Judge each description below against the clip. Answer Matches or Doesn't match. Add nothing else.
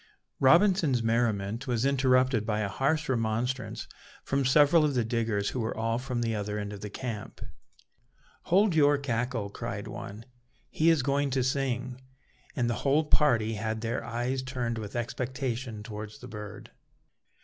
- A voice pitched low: Matches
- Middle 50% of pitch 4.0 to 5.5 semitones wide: Doesn't match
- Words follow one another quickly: Doesn't match